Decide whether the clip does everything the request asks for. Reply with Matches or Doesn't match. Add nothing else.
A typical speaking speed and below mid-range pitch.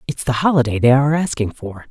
Doesn't match